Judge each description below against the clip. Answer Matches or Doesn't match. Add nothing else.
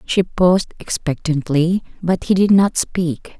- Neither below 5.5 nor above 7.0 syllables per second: Doesn't match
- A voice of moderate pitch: Matches